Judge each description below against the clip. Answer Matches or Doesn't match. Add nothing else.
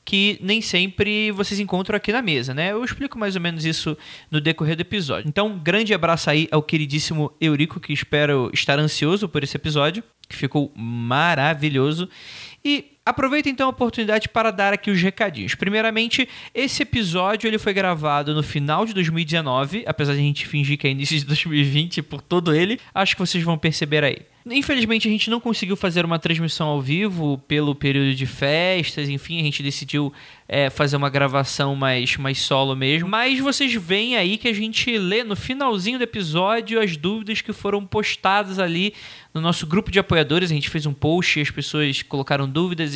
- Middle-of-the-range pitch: Matches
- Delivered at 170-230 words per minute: Matches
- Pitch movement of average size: Doesn't match